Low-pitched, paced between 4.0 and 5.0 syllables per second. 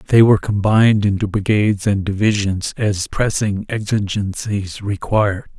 Yes: low, 105 Hz; 4.7 syllables/s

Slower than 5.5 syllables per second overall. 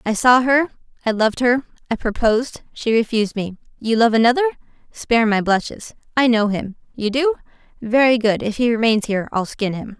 No: 5.7 syllables/s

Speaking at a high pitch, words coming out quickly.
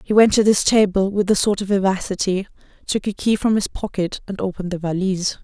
Yes: high, 195 Hz; fast, 220 wpm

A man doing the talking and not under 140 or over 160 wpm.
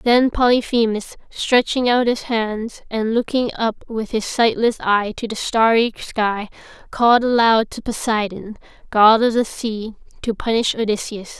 No: female; average, 145 wpm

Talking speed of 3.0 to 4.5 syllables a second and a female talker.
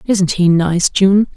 Yes: 3.3 syllables/s; female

